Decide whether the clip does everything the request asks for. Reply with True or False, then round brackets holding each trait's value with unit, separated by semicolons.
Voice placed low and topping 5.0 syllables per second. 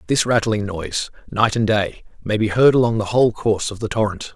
True (110 Hz; 5.8 syllables/s)